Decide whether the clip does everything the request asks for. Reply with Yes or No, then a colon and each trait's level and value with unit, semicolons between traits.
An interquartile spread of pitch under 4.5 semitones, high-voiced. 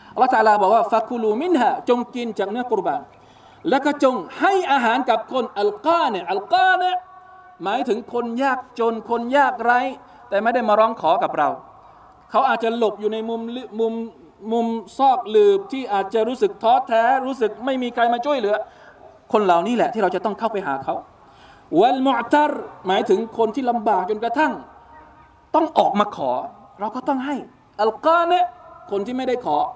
No: average, 5.0 semitones; high, 245 Hz